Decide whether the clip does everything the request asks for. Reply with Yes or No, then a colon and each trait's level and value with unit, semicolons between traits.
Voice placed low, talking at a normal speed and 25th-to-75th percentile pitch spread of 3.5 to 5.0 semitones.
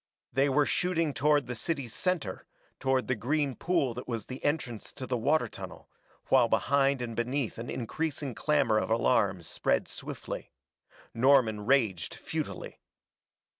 Yes: low, 130 Hz; average, 145 wpm; average, 4.0 semitones